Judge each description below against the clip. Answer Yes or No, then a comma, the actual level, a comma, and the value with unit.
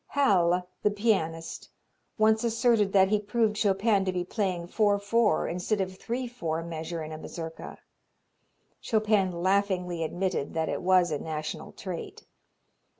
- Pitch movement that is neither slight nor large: Yes, average, 3.8 semitones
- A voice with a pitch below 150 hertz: No, high, 190 Hz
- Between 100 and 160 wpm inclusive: Yes, average, 145 wpm